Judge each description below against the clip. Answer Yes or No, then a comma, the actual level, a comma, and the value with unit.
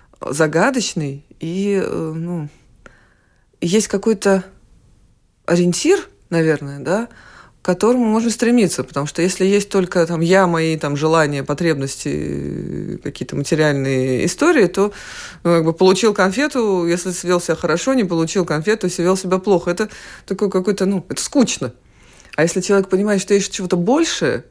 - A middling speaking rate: Yes, average, 140 wpm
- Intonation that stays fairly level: No, average, 3.9 semitones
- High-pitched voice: No, medium, 180 Hz